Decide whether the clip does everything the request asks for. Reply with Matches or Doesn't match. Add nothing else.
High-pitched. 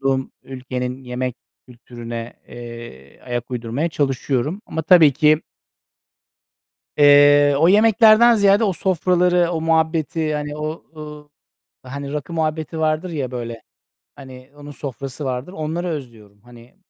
Doesn't match